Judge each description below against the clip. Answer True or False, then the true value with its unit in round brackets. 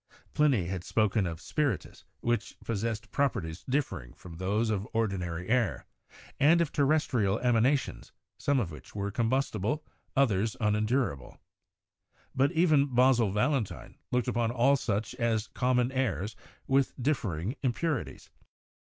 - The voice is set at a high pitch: False (115 Hz)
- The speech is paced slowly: True (130 wpm)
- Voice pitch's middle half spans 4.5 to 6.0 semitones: True (5.0 semitones)